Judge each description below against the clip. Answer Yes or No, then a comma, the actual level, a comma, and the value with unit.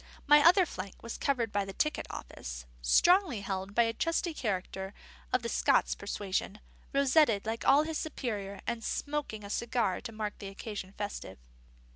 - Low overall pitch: No, high, 220 Hz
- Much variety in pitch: Yes, wide, 5.9 semitones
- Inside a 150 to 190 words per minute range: Yes, average, 160 wpm